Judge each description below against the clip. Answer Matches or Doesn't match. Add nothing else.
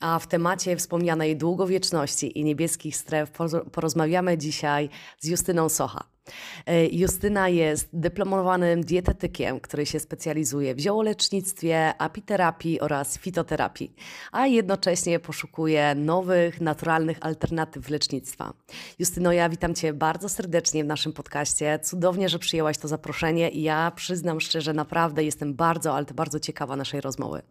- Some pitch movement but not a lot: Doesn't match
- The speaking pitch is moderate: Matches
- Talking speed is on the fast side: Doesn't match